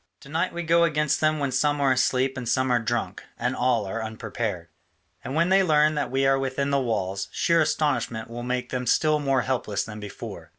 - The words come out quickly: Yes, fast, 215 wpm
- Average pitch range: Yes, average, 4.3 semitones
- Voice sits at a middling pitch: No, low, 130 Hz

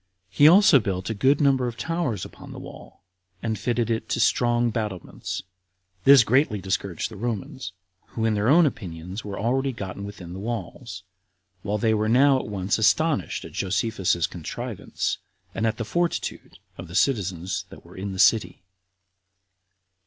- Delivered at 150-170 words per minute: Yes, average, 165 wpm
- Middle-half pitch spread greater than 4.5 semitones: Yes, average, 4.9 semitones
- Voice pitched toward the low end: Yes, low, 110 Hz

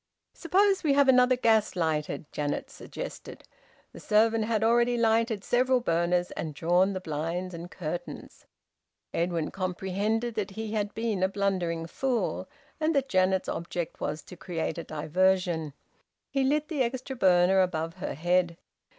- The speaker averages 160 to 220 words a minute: No, average, 150 wpm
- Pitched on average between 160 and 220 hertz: Yes, high, 190 Hz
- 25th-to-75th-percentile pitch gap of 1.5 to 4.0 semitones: No, wide, 5.4 semitones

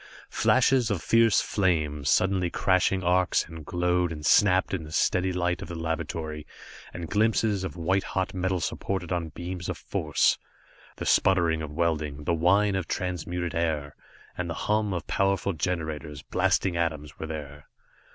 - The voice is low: Yes, very low, 90 Hz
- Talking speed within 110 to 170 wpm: Yes, average, 160 wpm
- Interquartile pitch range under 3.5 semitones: Yes, average, 2.9 semitones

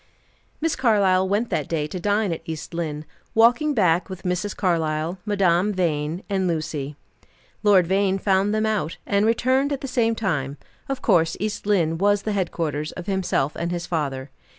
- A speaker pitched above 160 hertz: Yes, medium, 185 Hz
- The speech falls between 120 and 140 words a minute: No, average, 175 wpm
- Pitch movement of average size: Yes, average, 4.2 semitones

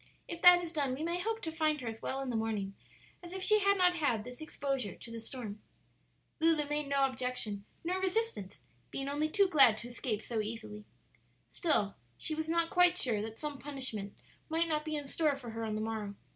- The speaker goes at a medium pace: No, fast, 215 wpm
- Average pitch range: No, wide, 6.7 semitones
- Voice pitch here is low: No, very high, 280 Hz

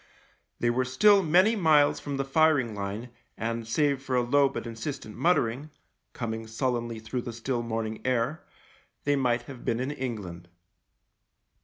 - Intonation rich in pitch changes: No, average, 3.8 semitones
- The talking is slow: No, average, 155 wpm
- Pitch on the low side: Yes, low, 125 Hz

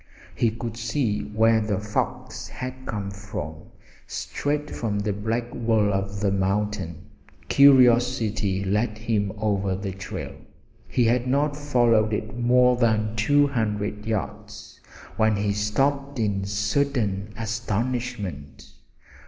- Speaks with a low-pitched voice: Yes, low, 110 Hz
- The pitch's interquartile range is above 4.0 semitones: No, average, 2.9 semitones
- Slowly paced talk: Yes, slow, 120 wpm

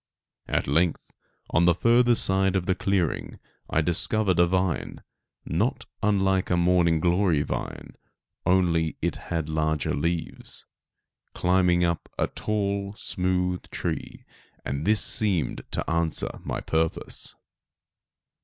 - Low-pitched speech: Yes, very low, 90 Hz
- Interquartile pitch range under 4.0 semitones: Yes, average, 2.7 semitones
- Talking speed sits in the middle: No, slow, 120 wpm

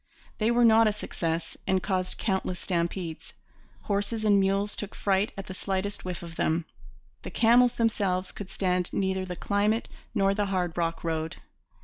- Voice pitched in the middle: No, high, 195 Hz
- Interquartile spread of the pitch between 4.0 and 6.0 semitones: No, narrow, 2.5 semitones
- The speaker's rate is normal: Yes, average, 165 wpm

